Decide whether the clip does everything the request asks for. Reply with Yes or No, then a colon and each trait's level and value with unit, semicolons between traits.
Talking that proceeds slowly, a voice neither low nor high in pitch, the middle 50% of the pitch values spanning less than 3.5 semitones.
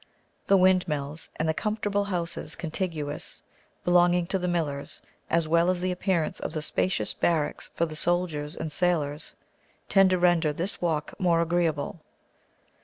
No: average, 150 wpm; medium, 170 Hz; narrow, 2.6 semitones